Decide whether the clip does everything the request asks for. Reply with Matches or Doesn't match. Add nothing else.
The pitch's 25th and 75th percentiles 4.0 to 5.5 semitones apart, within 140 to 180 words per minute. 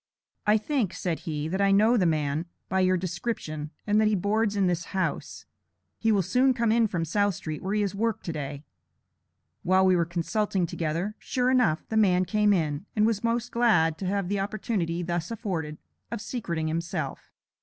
Doesn't match